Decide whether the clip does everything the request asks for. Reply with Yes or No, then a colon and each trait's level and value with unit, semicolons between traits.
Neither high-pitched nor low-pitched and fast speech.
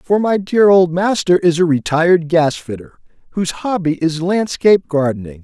No: medium, 170 Hz; average, 165 wpm